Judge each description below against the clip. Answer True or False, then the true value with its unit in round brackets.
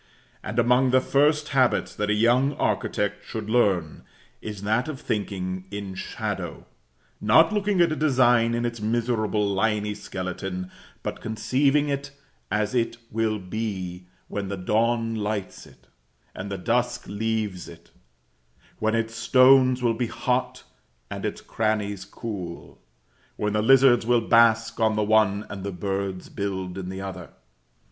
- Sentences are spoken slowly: False (150 wpm)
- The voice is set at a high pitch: False (110 Hz)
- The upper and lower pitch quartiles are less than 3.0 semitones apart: False (3.4 semitones)